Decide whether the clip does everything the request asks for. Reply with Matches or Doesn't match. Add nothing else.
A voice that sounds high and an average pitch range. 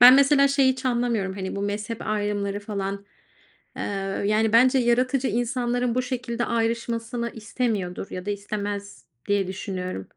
Matches